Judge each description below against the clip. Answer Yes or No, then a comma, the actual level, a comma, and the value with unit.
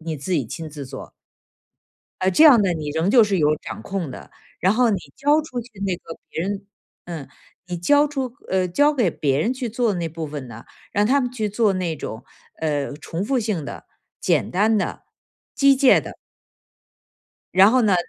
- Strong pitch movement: Yes, wide, 7.0 semitones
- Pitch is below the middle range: No, high, 190 Hz